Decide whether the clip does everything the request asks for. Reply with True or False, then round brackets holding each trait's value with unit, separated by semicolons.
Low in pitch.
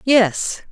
False (215 Hz)